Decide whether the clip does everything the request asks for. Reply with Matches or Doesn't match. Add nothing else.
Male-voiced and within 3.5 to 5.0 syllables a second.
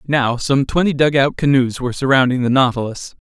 Doesn't match